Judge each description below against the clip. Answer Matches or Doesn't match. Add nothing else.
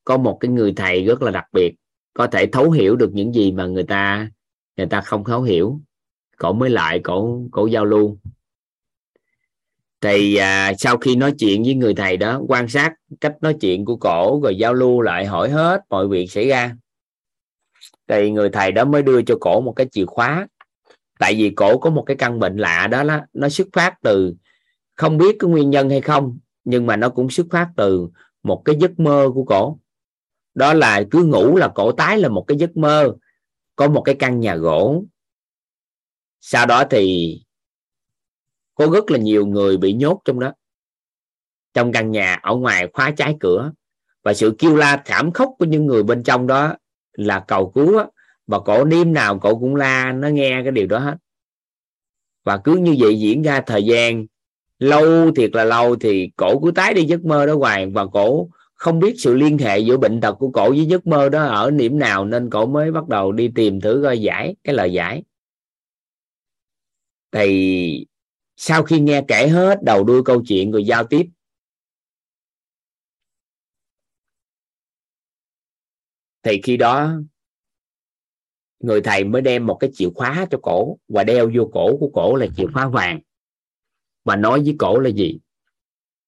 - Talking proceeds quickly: Doesn't match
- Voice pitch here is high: Doesn't match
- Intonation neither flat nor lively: Doesn't match